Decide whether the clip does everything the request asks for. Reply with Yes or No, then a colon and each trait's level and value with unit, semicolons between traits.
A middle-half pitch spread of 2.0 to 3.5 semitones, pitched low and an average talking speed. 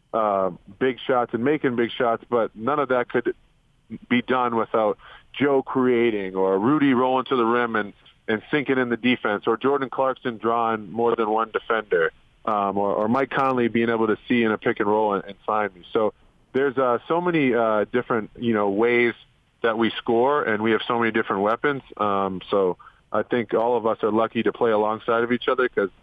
No: average, 3.0 semitones; low, 115 Hz; fast, 210 wpm